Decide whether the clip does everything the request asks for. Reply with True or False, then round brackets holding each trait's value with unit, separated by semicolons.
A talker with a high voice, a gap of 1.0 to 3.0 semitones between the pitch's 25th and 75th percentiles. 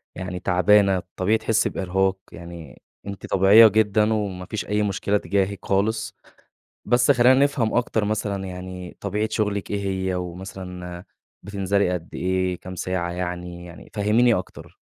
False (95 Hz; 2.6 semitones)